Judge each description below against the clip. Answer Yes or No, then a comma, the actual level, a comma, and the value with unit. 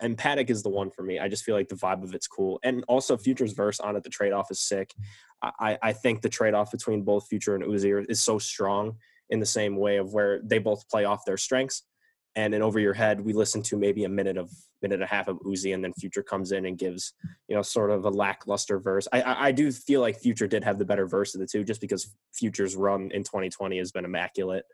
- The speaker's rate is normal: No, fast, 260 wpm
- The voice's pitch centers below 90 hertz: No, low, 100 Hz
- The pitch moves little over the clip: Yes, narrow, 2.1 semitones